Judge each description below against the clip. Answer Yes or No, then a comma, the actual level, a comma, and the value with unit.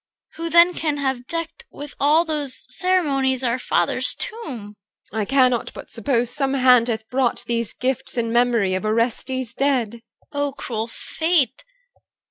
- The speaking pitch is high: Yes, very high, 260 Hz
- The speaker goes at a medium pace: Yes, average, 155 wpm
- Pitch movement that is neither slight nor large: Yes, average, 3.7 semitones